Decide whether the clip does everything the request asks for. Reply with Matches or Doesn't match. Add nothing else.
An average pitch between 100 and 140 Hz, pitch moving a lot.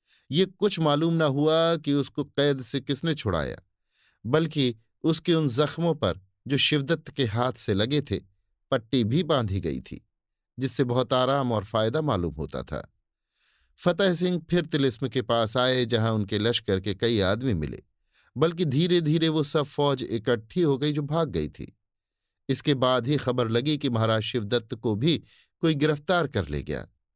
Matches